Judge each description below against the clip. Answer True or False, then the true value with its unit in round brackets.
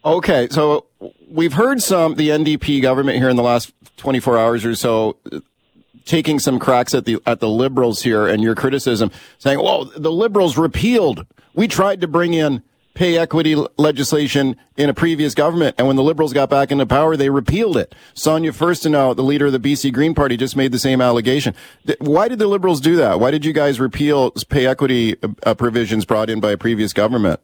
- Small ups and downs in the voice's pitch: False (4.3 semitones)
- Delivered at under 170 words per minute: False (200 wpm)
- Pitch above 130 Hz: True (140 Hz)